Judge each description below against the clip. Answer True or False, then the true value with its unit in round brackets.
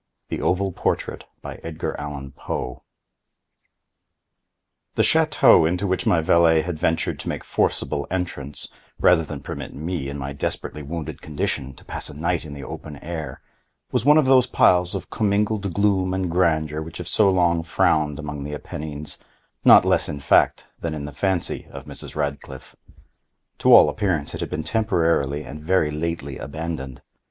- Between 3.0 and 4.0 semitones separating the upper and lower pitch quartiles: True (3.7 semitones)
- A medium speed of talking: True (160 wpm)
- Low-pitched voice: True (80 Hz)